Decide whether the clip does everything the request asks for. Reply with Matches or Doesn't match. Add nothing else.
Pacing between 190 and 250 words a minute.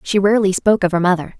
Doesn't match